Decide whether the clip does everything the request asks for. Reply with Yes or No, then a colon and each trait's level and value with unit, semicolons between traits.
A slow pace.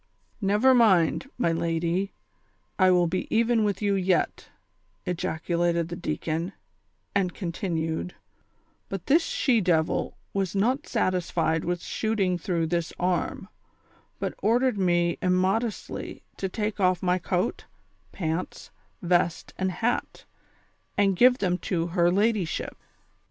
Yes: slow, 125 wpm